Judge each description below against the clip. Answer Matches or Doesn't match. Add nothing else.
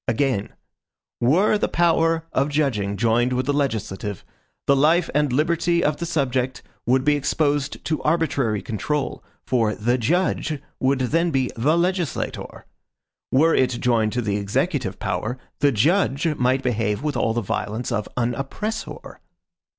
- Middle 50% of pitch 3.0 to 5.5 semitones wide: Matches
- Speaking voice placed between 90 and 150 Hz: Matches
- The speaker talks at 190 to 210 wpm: Doesn't match